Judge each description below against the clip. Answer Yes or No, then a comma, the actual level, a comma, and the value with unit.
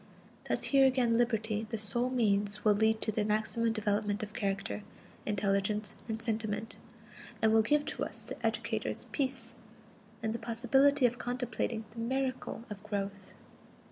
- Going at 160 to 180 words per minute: No, average, 150 wpm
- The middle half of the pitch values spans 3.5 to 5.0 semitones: No, narrow, 2.5 semitones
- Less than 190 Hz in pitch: No, high, 220 Hz